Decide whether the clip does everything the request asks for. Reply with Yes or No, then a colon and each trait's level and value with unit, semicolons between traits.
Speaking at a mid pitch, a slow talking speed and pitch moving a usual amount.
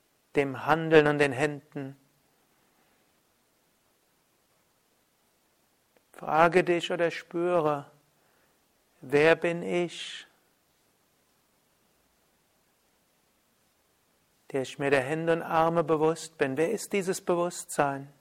Yes: medium, 155 Hz; slow, 80 wpm; average, 3.2 semitones